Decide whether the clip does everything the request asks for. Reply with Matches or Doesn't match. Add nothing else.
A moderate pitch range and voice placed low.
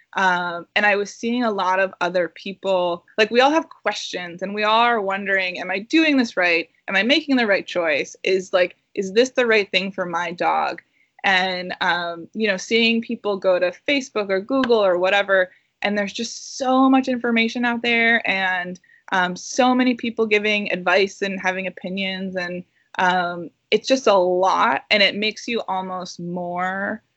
Doesn't match